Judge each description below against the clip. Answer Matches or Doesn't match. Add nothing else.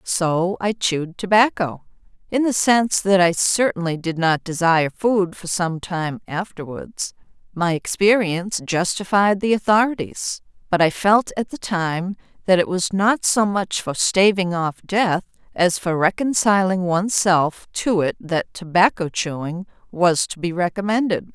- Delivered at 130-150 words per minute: Matches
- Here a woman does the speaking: Matches